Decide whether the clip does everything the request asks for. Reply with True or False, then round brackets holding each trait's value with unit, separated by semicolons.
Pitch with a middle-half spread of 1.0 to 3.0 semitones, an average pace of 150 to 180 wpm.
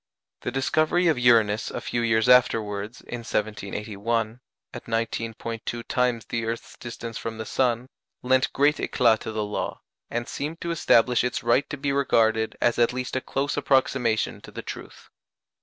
True (2.5 semitones; 165 wpm)